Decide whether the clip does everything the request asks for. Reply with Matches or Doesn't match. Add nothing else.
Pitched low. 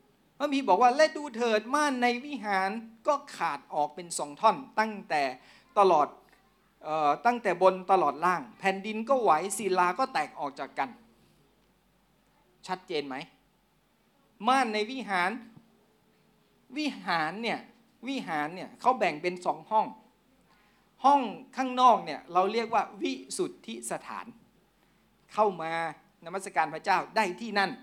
Doesn't match